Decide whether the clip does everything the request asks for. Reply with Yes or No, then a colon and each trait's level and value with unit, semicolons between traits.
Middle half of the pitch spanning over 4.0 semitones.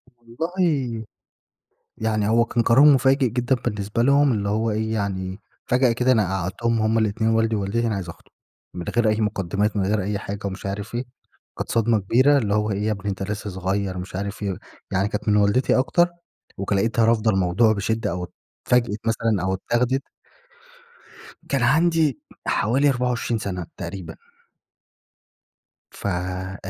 No: average, 3.3 semitones